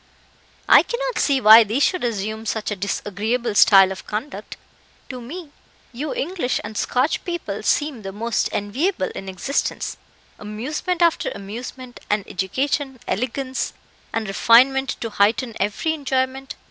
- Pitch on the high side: Yes, high, 240 Hz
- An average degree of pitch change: Yes, average, 4.8 semitones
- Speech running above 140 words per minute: No, slow, 135 wpm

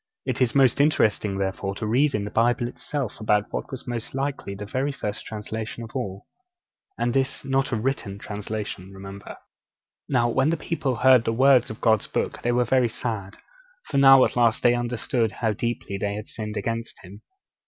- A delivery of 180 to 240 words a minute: Yes, average, 190 wpm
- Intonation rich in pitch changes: No, average, 3.8 semitones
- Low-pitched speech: Yes, low, 115 Hz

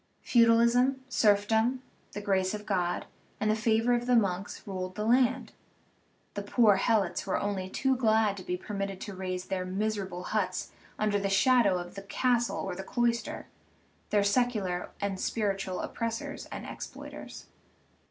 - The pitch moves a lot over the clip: No, average, 3.4 semitones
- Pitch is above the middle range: Yes, high, 205 Hz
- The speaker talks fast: No, average, 160 wpm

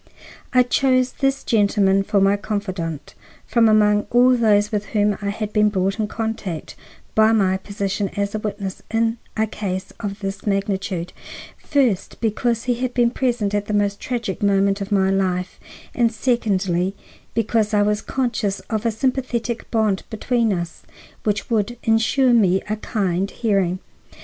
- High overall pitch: Yes, high, 210 Hz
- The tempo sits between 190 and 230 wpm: No, average, 155 wpm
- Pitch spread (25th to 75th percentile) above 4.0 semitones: No, average, 2.7 semitones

